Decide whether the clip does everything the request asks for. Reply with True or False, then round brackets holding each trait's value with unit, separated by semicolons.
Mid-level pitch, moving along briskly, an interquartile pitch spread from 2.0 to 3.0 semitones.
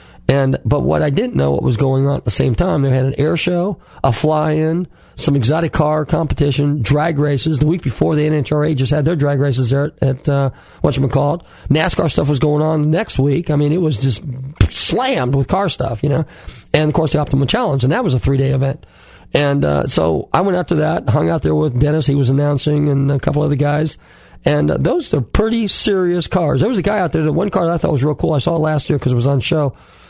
True (145 Hz; 255 wpm; 2.6 semitones)